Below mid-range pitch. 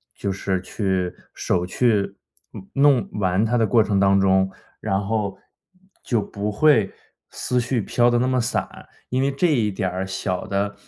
Yes: low, 100 Hz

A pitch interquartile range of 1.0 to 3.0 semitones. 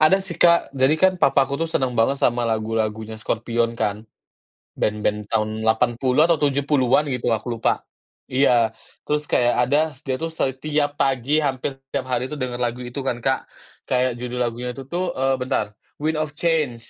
No: average, 3.7 semitones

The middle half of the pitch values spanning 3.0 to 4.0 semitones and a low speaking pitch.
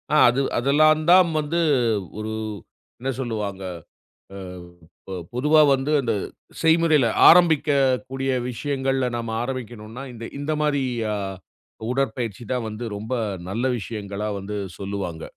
No: average, 4.8 semitones; low, 130 Hz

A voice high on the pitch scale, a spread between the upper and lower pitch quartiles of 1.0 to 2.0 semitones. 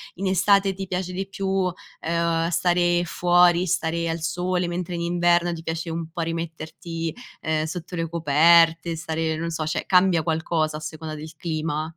No: medium, 170 Hz; narrow, 1.5 semitones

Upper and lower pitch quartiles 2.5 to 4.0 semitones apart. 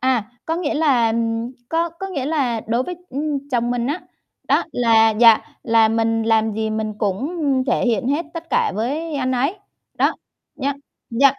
No: average, 4.6 semitones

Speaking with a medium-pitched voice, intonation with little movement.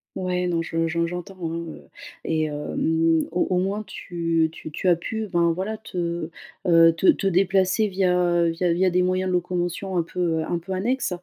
Yes: medium, 175 Hz; narrow, 2.0 semitones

